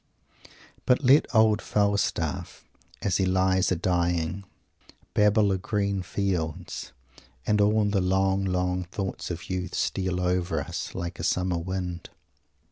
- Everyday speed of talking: No, slow, 130 wpm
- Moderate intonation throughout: No, narrow, 2.0 semitones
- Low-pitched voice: Yes, very low, 95 Hz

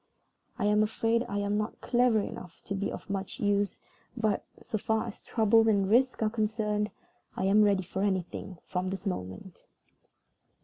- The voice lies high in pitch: Yes, high, 205 Hz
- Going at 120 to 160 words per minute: No, average, 170 wpm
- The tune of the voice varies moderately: No, narrow, 2.0 semitones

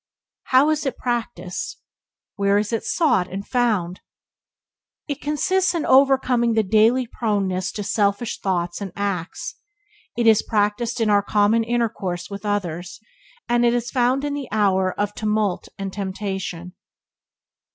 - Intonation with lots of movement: No, average, 3.7 semitones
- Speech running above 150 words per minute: No, average, 140 wpm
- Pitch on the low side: No, high, 210 Hz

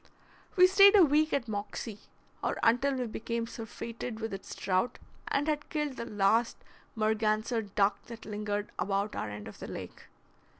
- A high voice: Yes, high, 225 Hz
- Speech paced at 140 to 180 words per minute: Yes, average, 165 wpm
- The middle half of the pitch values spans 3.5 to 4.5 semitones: Yes, average, 4.1 semitones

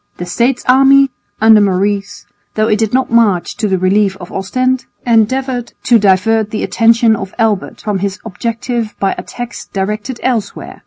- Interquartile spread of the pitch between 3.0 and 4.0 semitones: Yes, average, 3.4 semitones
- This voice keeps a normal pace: Yes, average, 160 wpm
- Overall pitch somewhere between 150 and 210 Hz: No, high, 220 Hz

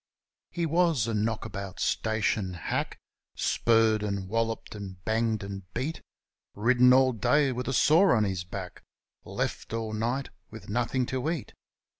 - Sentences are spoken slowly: No, average, 150 wpm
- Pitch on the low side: Yes, low, 115 Hz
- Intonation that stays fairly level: No, average, 3.9 semitones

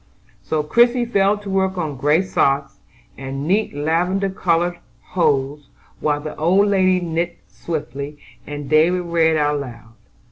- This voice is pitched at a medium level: Yes, medium, 165 Hz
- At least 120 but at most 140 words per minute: Yes, slow, 135 wpm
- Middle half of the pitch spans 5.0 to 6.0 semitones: No, average, 4.3 semitones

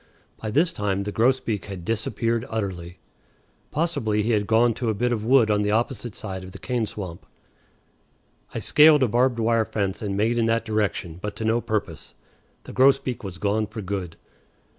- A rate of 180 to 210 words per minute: Yes, average, 185 wpm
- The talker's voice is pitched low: Yes, low, 110 Hz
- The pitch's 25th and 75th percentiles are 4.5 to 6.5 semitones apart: No, average, 2.8 semitones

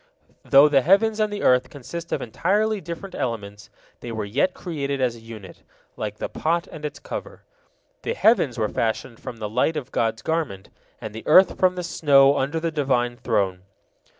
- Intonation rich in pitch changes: Yes, wide, 6.7 semitones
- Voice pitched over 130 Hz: Yes, medium, 140 Hz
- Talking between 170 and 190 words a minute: Yes, average, 185 wpm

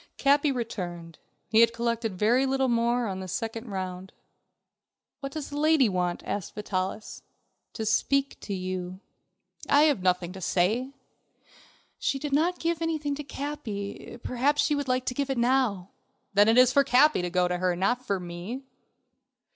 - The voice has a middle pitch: No, high, 235 Hz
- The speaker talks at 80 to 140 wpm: No, average, 170 wpm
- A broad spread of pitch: Yes, wide, 6.7 semitones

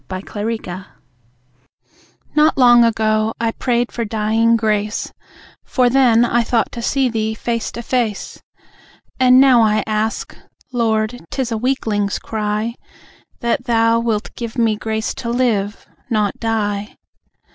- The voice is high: Yes, high, 225 Hz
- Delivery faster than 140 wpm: No, slow, 135 wpm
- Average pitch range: No, narrow, 1.9 semitones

